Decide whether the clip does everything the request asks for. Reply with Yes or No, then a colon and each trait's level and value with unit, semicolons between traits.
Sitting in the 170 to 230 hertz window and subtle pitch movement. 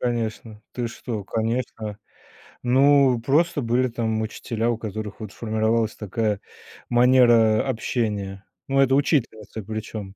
No: low, 115 Hz; narrow, 2.3 semitones